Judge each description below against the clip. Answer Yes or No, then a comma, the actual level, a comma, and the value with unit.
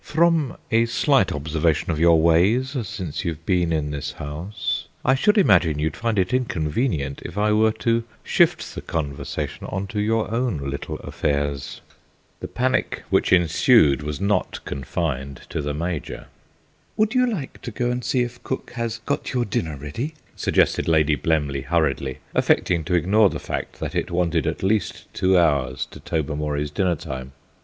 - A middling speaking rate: Yes, average, 165 wpm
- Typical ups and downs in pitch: No, wide, 7.4 semitones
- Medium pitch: No, very low, 85 Hz